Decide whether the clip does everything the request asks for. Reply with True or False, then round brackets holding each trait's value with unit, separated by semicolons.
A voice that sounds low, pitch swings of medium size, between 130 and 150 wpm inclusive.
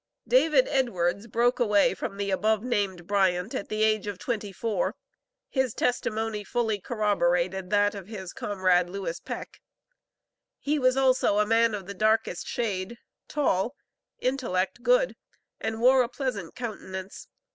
False (210 Hz; 4.0 semitones; 145 wpm)